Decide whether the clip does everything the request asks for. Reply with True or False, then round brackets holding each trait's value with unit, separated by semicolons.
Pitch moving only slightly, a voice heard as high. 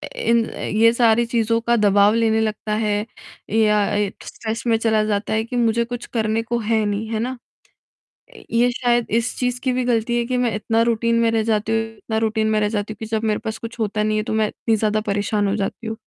True (1.5 semitones; 225 Hz)